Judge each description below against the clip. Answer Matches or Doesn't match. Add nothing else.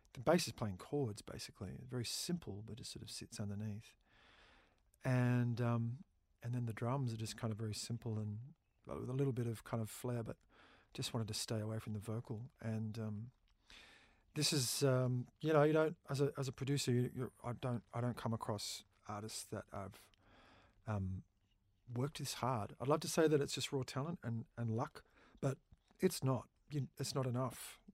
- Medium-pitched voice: Doesn't match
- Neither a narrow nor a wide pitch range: Matches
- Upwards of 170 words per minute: Matches